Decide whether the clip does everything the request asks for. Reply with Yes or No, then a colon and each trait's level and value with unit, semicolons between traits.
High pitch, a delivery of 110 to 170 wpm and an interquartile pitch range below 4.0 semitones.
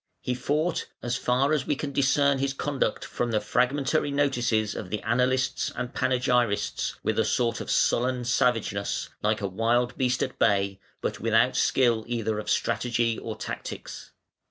No: low, 125 Hz; average, 160 wpm; average, 2.9 semitones